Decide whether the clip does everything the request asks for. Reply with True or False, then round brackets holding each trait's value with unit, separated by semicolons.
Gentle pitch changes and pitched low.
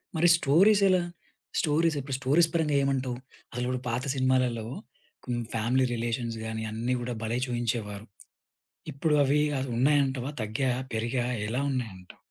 False (3.0 semitones; 125 Hz)